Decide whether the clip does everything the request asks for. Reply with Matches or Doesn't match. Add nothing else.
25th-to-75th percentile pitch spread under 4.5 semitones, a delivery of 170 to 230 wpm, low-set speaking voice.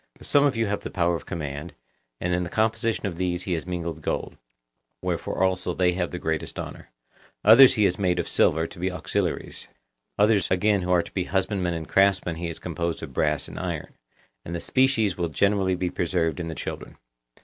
Matches